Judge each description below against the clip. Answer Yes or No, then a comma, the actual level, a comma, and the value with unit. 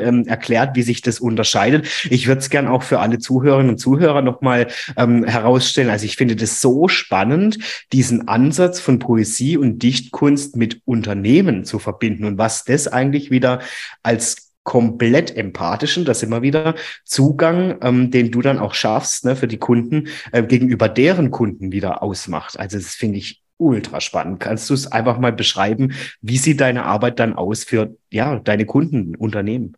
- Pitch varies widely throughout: No, average, 2.9 semitones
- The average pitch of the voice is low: Yes, low, 125 Hz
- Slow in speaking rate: No, average, 170 wpm